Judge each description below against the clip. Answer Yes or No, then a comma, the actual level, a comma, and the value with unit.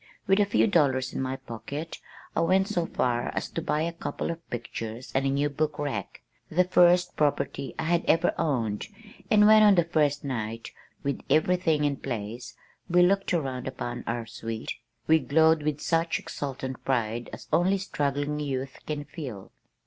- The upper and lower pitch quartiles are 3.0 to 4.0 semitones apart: No, average, 4.6 semitones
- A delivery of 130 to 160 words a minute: No, average, 175 wpm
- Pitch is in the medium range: Yes, medium, 145 Hz